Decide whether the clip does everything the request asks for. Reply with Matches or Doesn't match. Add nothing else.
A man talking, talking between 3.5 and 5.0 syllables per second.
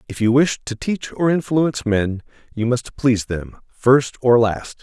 Matches